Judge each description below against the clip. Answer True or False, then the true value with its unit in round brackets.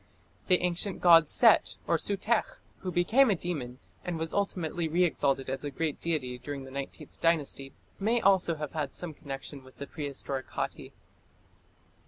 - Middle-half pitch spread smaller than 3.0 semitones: False (4.5 semitones)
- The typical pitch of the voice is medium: True (160 Hz)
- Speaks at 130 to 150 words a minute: False (160 wpm)